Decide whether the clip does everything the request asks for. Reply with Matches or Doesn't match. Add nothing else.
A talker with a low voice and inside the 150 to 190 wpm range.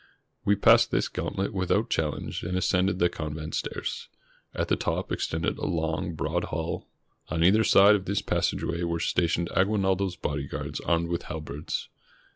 Matches